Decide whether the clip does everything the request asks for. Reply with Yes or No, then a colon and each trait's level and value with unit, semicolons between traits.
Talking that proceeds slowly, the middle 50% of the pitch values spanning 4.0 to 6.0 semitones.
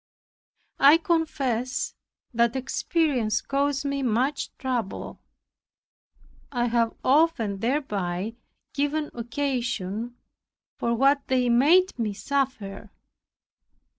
No: slow, 85 wpm; average, 3.6 semitones